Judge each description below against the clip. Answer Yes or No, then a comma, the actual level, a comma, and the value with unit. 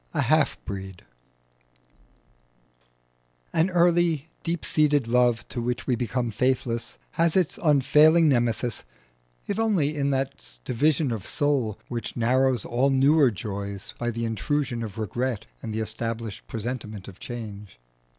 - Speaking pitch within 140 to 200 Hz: No, low, 125 Hz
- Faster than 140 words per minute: No, slow, 135 wpm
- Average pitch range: Yes, average, 4.5 semitones